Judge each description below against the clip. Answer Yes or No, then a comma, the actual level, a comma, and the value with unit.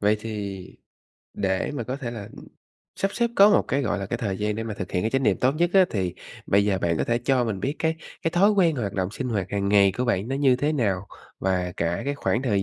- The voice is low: Yes, low, 110 Hz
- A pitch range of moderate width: No, wide, 5.8 semitones